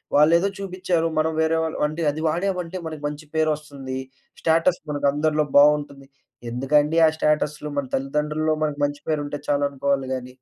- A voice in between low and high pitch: Yes, medium, 150 Hz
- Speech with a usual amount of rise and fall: No, narrow, 1.9 semitones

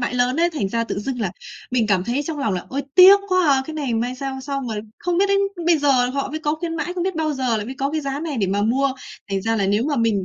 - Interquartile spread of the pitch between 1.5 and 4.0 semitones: No, wide, 5.5 semitones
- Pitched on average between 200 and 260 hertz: No, very high, 270 Hz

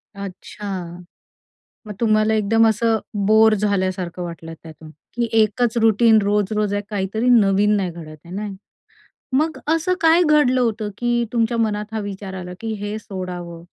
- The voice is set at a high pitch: Yes, high, 210 Hz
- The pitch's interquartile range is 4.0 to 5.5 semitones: No, average, 2.9 semitones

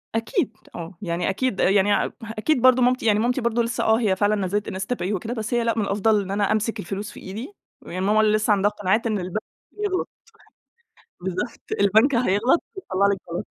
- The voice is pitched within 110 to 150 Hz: No, high, 215 Hz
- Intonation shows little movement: No, average, 3.2 semitones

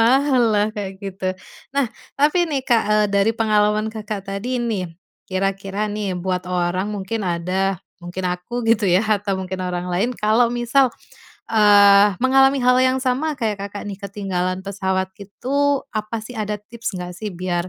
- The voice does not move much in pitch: No, average, 3.8 semitones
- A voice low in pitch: No, high, 205 Hz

